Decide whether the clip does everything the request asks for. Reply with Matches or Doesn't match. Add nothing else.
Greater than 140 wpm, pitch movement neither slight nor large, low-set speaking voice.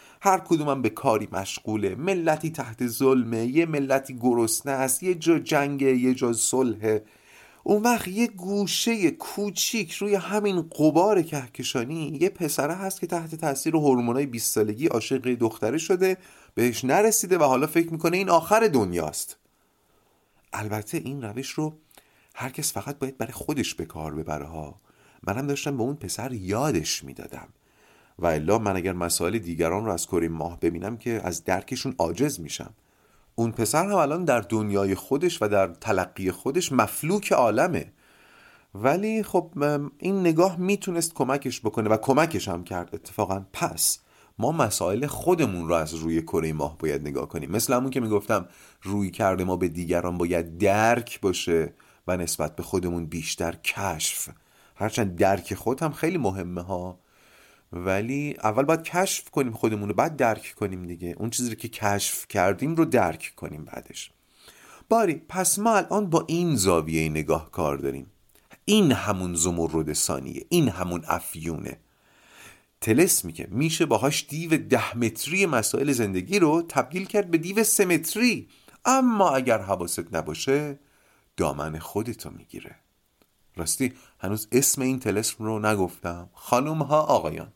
Doesn't match